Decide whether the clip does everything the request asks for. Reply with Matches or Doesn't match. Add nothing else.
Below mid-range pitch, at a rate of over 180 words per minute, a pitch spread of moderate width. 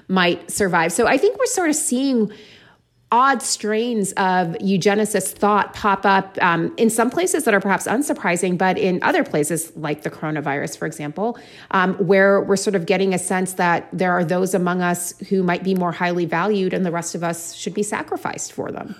Doesn't match